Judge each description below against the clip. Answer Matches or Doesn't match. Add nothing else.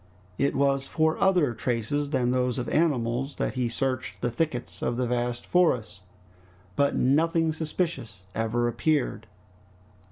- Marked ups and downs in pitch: Doesn't match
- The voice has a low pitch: Matches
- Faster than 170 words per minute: Doesn't match